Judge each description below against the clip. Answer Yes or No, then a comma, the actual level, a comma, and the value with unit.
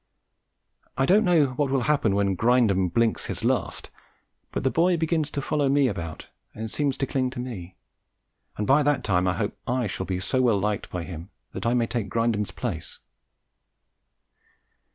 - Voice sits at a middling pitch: No, low, 120 Hz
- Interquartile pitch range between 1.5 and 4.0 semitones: No, wide, 5.6 semitones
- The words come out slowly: No, average, 180 wpm